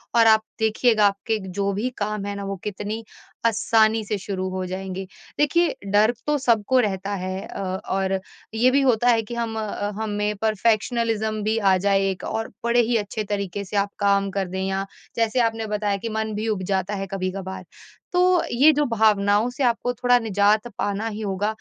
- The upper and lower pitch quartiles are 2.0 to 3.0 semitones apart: Yes, narrow, 2.4 semitones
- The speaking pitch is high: Yes, high, 210 Hz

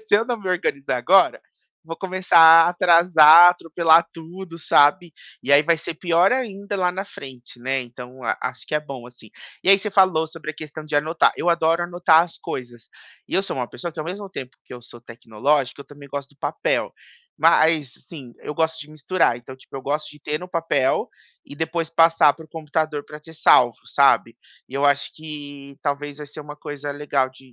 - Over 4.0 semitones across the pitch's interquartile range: No, average, 3.5 semitones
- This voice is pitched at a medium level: Yes, medium, 155 Hz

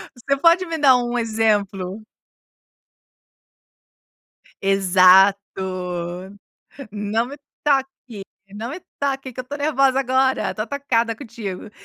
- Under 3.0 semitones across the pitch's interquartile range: No, average, 4.8 semitones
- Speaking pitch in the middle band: No, high, 240 Hz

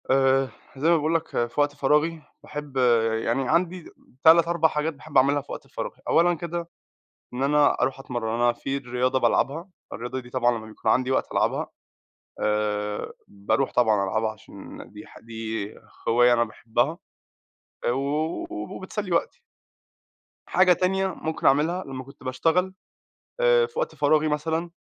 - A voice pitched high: No, medium, 140 Hz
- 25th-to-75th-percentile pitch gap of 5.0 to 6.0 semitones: Yes, average, 5.3 semitones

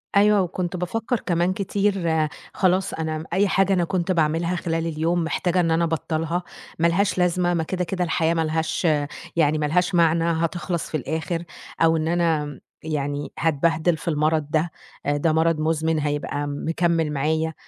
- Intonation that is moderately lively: No, narrow, 2.0 semitones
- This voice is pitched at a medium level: Yes, medium, 165 Hz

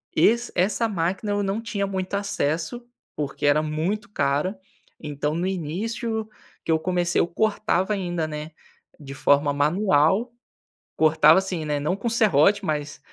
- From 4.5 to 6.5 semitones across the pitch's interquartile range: Yes, average, 5.1 semitones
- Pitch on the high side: No, medium, 175 Hz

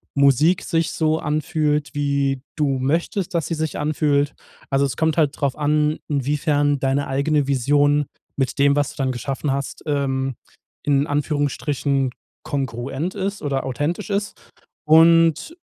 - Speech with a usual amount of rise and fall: No, narrow, 2.1 semitones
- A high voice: No, medium, 145 Hz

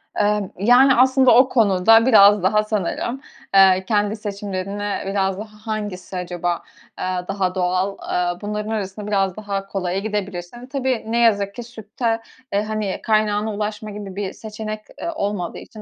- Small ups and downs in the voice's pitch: Yes, narrow, 2.2 semitones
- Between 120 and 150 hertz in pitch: No, high, 205 Hz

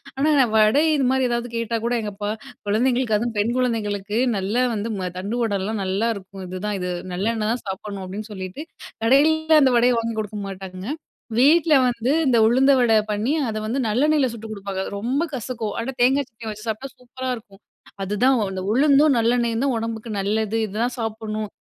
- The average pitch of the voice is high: Yes, high, 225 Hz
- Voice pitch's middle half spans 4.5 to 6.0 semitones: No, average, 3.3 semitones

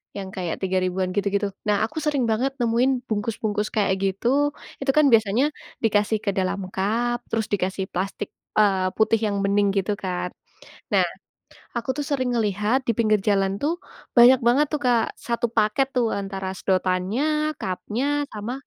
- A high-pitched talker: Yes, high, 210 Hz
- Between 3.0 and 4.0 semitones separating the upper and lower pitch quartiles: Yes, average, 3.6 semitones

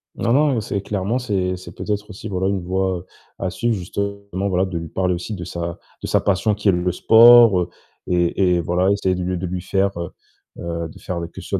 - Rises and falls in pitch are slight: Yes, narrow, 2.2 semitones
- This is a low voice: Yes, very low, 95 Hz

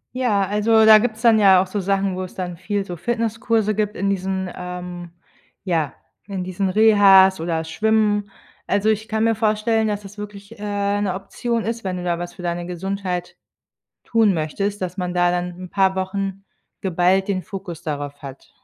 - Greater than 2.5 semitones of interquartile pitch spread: Yes, average, 2.9 semitones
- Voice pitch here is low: No, high, 195 Hz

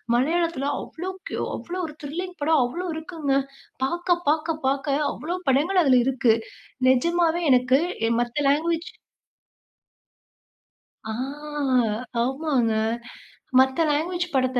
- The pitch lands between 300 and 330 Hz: Yes, very high, 305 Hz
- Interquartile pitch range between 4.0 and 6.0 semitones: Yes, average, 4.5 semitones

